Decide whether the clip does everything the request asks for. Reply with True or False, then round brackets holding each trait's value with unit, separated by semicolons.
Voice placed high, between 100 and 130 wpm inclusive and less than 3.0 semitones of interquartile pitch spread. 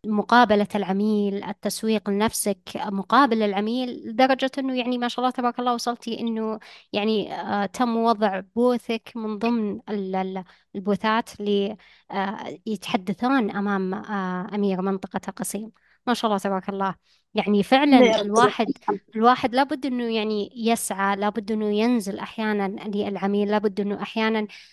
True (215 Hz; 120 wpm; 2.5 semitones)